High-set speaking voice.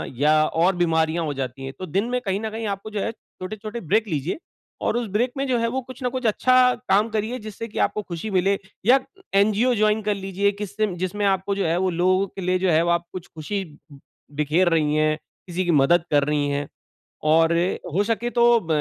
Yes: high, 195 Hz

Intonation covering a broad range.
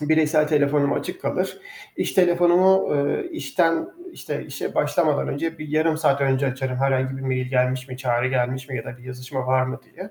No: average, 3.5 semitones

